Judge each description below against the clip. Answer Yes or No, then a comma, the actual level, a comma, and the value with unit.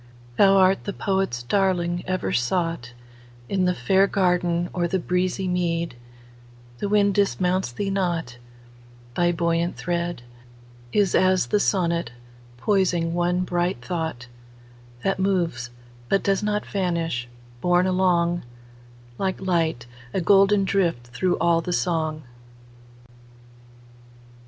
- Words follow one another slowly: Yes, slow, 105 wpm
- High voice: No, medium, 170 Hz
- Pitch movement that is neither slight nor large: No, wide, 7.5 semitones